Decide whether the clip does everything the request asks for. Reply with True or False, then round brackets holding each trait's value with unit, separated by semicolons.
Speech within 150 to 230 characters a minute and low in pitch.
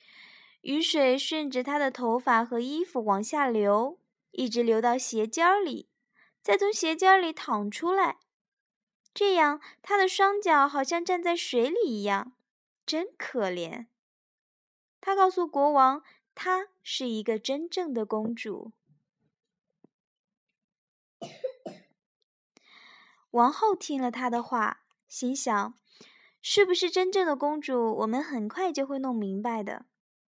False (175 characters per minute; 270 Hz)